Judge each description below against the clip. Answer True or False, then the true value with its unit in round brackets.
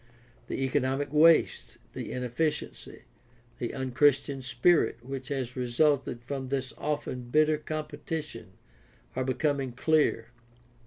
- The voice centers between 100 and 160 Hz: True (135 Hz)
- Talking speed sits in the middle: False (110 wpm)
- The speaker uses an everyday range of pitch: True (3.0 semitones)